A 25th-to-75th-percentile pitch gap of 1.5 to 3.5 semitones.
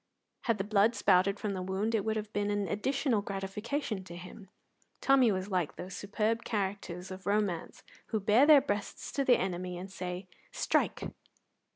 Yes: average, 2.8 semitones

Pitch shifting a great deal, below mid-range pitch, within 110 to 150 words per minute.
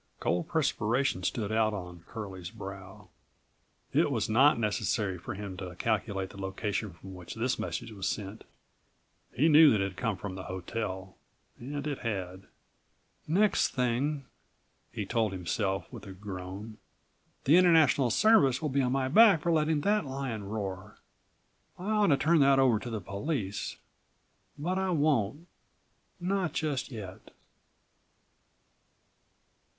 Yes: wide, 6.9 semitones; low, 115 Hz; average, 145 wpm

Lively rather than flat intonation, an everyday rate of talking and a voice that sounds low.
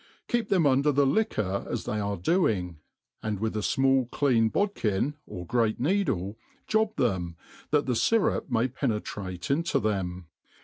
Yes: wide, 6.5 semitones; average, 165 wpm; low, 120 Hz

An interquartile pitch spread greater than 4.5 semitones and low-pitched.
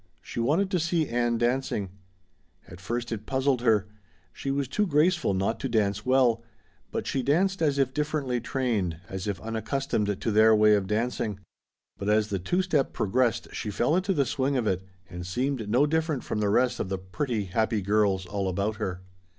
Yes: average, 5.1 semitones; low, 115 Hz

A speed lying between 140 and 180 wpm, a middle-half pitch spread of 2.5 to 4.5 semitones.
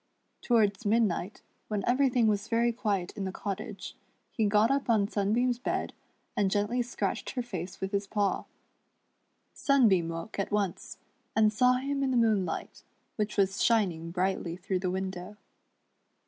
Yes: average, 155 wpm; average, 3.5 semitones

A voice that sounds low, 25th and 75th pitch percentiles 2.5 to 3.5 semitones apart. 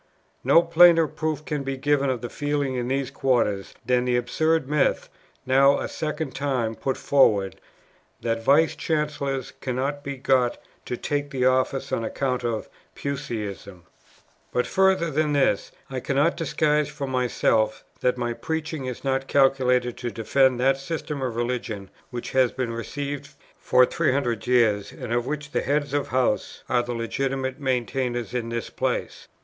Yes: low, 130 Hz; average, 2.9 semitones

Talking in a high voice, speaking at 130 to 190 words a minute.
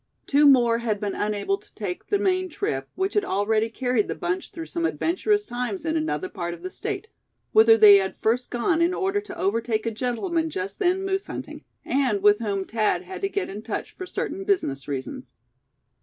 No: very high, 250 Hz; average, 200 wpm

